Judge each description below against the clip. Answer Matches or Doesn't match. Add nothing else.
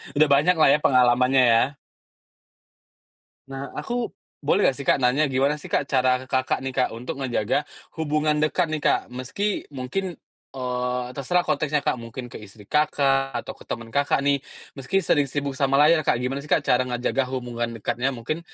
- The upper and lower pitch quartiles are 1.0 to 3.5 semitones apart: Matches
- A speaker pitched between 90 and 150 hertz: Matches